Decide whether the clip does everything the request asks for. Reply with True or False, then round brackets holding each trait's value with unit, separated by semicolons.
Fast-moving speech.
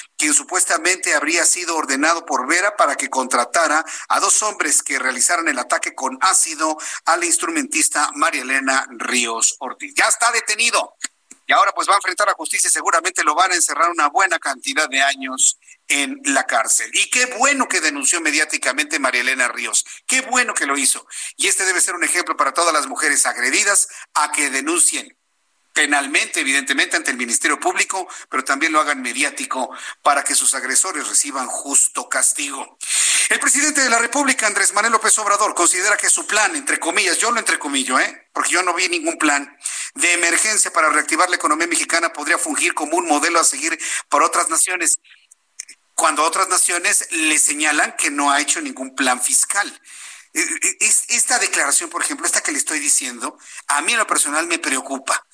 False (180 wpm)